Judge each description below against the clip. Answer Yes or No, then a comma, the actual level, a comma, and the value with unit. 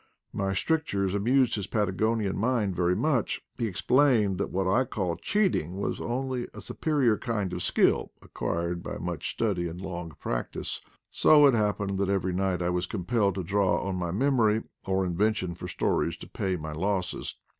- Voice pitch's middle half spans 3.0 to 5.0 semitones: Yes, average, 4.2 semitones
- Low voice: Yes, low, 100 Hz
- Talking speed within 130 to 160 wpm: No, average, 180 wpm